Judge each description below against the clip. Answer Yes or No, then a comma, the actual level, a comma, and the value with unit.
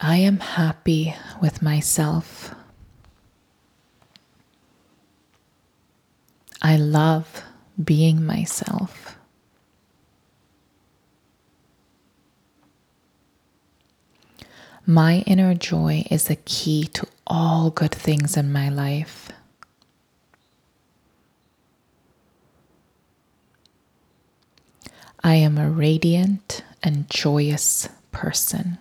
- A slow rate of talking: Yes, slow, 60 wpm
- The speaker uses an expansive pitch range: No, narrow, 2.4 semitones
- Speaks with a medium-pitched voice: Yes, medium, 155 Hz